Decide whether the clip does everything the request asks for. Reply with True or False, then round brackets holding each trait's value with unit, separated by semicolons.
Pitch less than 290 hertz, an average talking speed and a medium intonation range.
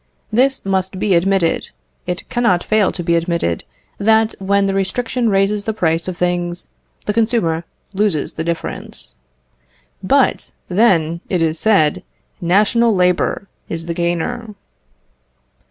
False (190 Hz; 130 wpm; 3.9 semitones)